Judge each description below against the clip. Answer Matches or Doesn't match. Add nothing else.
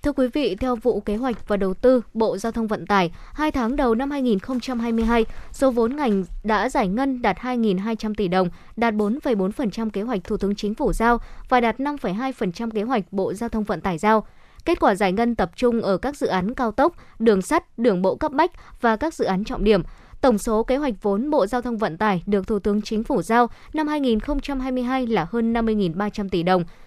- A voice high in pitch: Matches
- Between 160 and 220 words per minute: Matches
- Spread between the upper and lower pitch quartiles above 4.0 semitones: Doesn't match